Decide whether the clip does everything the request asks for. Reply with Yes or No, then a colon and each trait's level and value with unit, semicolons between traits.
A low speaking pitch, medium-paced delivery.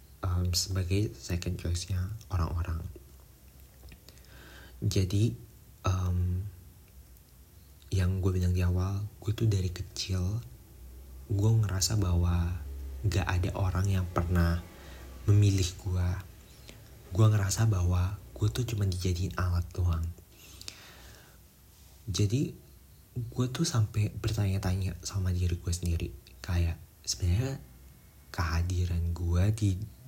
Yes: very low, 90 Hz; average, 100 wpm